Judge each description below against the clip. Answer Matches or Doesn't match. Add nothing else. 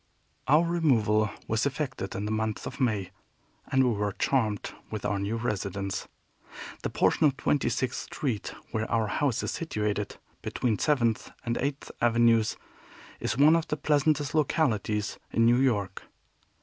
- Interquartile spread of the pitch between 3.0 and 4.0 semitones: Doesn't match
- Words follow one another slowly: Doesn't match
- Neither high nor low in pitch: Doesn't match